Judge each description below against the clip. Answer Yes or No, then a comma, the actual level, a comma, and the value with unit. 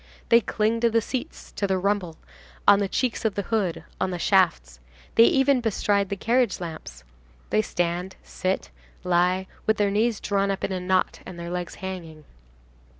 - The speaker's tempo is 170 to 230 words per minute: Yes, average, 180 wpm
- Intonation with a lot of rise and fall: No, average, 3.4 semitones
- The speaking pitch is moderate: No, high, 195 Hz